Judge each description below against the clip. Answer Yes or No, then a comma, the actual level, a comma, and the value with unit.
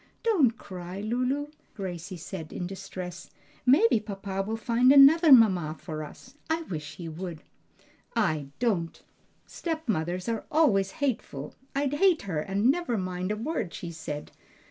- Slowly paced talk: No, average, 145 wpm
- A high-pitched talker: Yes, high, 200 Hz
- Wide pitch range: Yes, wide, 6.9 semitones